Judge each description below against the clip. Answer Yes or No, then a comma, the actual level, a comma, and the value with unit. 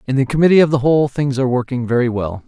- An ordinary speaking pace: No, fast, 265 wpm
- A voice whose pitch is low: Yes, low, 130 Hz